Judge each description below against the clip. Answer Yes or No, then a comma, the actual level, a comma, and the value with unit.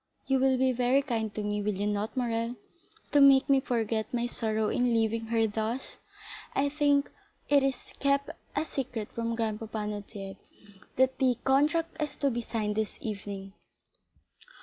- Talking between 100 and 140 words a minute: No, average, 165 wpm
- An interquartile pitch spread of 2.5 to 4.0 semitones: Yes, average, 3.7 semitones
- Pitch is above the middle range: Yes, high, 235 Hz